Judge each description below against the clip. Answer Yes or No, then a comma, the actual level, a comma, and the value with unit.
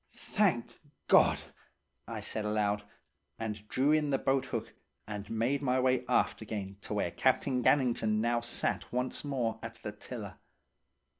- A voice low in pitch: Yes, low, 120 Hz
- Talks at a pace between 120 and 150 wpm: Yes, average, 145 wpm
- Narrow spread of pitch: No, average, 3.7 semitones